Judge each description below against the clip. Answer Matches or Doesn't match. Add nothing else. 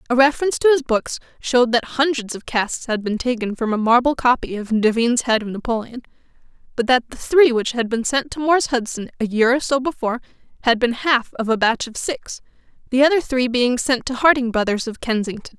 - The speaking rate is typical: Doesn't match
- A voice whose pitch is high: Matches